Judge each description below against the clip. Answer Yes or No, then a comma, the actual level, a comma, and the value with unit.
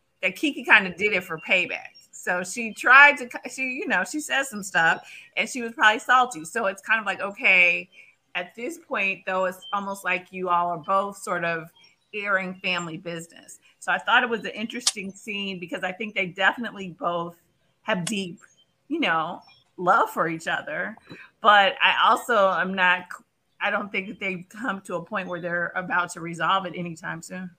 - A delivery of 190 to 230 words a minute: Yes, average, 195 wpm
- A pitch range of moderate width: Yes, average, 3.6 semitones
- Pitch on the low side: No, high, 195 Hz